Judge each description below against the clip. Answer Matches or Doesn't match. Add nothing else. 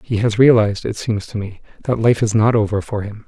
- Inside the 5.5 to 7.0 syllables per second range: Matches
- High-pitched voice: Doesn't match